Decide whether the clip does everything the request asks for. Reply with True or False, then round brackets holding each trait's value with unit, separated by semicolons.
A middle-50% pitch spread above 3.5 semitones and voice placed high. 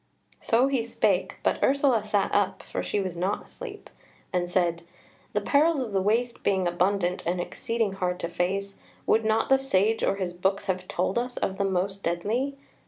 True (4.3 semitones; 200 Hz)